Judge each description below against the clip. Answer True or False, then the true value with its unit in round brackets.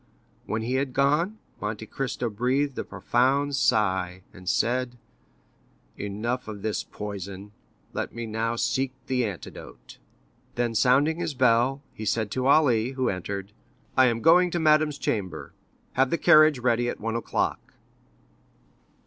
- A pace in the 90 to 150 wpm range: True (140 wpm)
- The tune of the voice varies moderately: True (4.2 semitones)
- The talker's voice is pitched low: True (120 Hz)